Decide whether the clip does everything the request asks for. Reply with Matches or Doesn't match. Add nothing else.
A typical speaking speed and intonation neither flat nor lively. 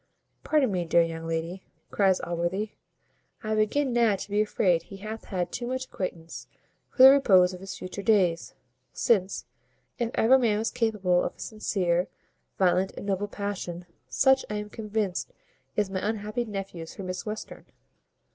Matches